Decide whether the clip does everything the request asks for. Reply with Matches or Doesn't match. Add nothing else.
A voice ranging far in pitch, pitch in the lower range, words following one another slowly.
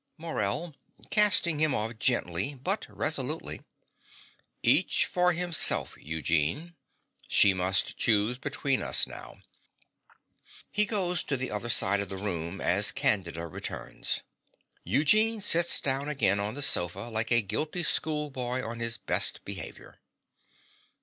Matches